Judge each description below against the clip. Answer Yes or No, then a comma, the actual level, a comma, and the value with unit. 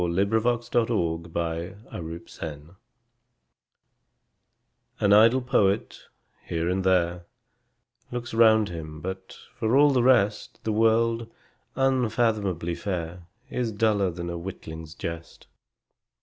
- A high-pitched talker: No, very low, 95 Hz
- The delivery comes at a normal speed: No, slow, 105 wpm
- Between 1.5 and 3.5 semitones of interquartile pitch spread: No, average, 5.0 semitones